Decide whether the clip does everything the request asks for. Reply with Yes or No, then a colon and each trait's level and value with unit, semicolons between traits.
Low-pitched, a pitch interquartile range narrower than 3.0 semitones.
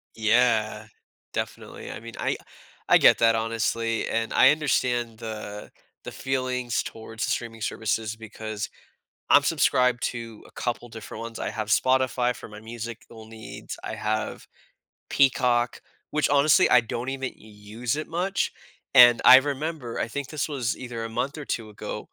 Yes: low, 115 Hz; narrow, 2.6 semitones